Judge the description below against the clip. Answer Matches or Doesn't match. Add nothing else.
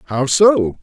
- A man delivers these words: Matches